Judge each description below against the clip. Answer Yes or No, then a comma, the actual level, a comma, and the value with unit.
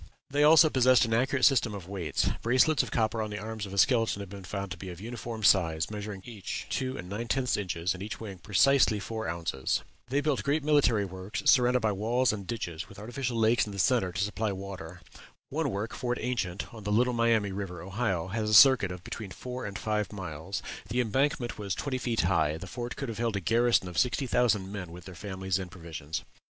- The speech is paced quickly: Yes, fast, 220 wpm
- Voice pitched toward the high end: No, low, 105 Hz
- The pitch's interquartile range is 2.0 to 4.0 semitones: No, average, 4.4 semitones